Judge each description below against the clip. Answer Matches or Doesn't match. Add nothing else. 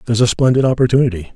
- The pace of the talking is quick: Doesn't match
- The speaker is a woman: Doesn't match